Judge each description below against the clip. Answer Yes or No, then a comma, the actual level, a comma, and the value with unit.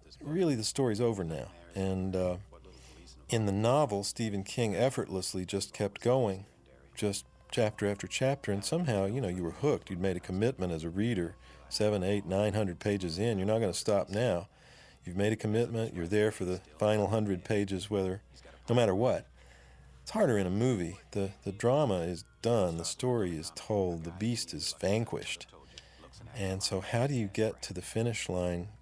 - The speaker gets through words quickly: No, average, 185 wpm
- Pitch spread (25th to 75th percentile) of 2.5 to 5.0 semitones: Yes, average, 3.9 semitones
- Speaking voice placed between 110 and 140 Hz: No, low, 100 Hz